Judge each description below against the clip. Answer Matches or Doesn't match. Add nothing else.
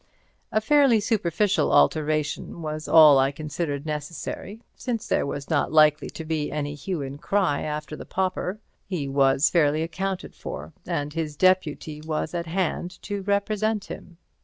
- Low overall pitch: Doesn't match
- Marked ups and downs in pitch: Doesn't match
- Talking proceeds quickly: Doesn't match